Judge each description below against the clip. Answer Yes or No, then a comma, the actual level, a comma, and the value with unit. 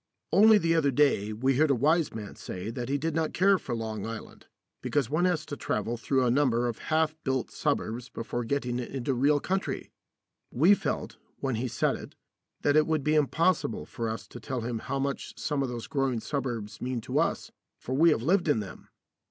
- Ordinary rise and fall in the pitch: Yes, average, 4.6 semitones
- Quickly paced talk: Yes, fast, 210 wpm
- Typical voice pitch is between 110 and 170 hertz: Yes, low, 135 Hz